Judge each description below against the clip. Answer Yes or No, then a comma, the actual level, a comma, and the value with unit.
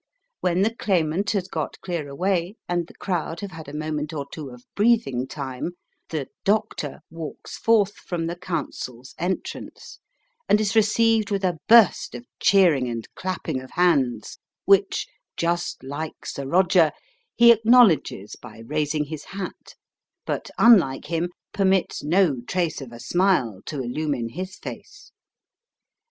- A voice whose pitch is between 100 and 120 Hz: No, medium, 170 Hz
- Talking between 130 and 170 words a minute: Yes, average, 145 wpm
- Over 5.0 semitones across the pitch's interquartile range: Yes, wide, 5.4 semitones